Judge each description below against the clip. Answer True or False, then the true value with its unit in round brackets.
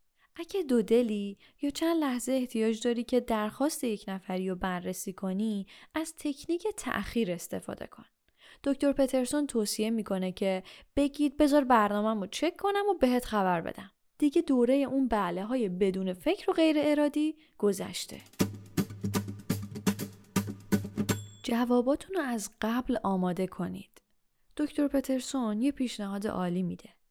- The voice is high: True (230 Hz)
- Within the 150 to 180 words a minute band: False (130 wpm)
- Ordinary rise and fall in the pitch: False (7.1 semitones)